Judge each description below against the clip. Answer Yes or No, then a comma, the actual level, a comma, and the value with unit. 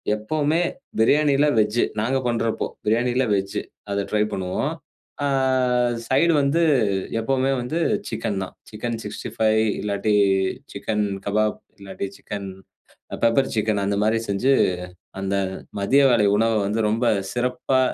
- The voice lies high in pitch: No, low, 110 Hz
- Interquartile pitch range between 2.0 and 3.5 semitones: No, average, 4.0 semitones